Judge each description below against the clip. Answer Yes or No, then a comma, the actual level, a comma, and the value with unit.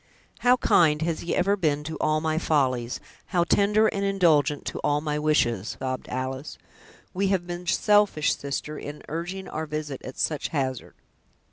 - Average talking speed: Yes, average, 165 wpm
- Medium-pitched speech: Yes, medium, 155 Hz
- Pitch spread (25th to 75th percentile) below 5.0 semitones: Yes, average, 3.8 semitones